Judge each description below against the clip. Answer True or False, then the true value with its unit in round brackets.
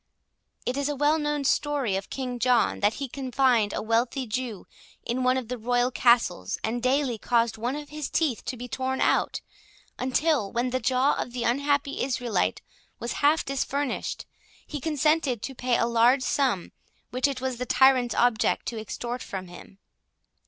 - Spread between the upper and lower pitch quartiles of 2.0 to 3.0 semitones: True (2.6 semitones)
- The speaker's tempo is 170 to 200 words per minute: True (175 wpm)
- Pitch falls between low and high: False (255 Hz)